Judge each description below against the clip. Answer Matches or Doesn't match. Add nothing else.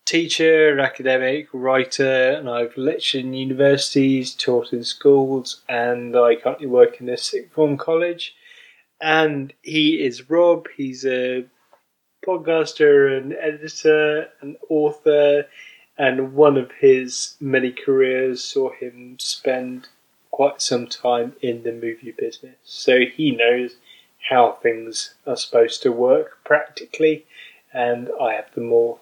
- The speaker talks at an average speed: Doesn't match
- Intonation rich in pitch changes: Doesn't match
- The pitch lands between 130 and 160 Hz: Matches